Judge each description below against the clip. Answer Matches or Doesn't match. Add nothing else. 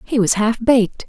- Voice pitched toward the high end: Matches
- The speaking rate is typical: Doesn't match